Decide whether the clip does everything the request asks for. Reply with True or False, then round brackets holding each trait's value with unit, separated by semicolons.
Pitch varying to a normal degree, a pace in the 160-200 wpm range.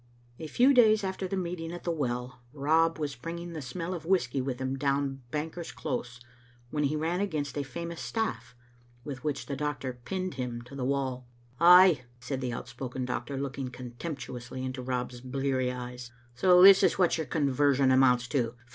True (4.7 semitones; 185 wpm)